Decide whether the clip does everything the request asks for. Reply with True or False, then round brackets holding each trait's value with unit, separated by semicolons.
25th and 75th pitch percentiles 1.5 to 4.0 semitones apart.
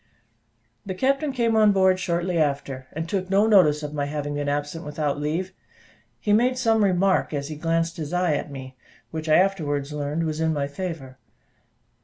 False (4.5 semitones)